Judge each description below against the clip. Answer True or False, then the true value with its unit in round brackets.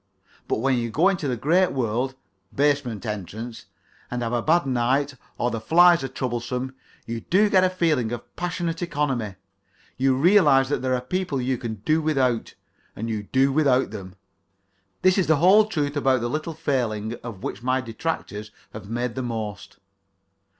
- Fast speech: False (175 wpm)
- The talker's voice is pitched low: True (130 Hz)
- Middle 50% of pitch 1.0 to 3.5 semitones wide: False (5.0 semitones)